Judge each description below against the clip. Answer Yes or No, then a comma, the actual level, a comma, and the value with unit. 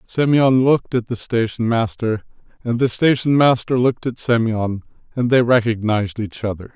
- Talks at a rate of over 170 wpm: No, average, 160 wpm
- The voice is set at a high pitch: No, low, 120 Hz